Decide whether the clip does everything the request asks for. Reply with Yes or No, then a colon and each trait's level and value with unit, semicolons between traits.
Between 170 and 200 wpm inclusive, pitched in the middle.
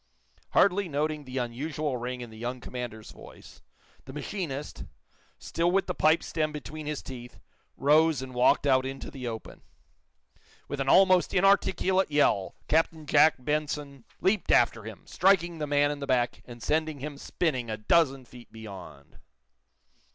No: average, 155 wpm; medium, 145 Hz